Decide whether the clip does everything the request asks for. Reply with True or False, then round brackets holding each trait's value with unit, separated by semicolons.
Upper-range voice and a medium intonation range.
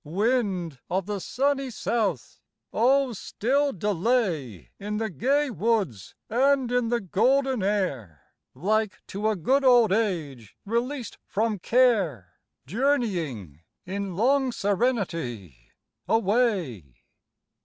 False (210 Hz; 6.7 semitones)